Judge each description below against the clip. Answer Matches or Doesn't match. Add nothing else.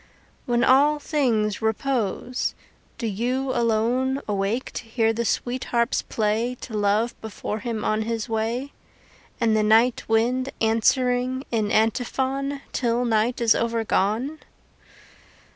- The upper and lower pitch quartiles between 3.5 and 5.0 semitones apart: Doesn't match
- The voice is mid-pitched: Doesn't match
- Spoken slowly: Matches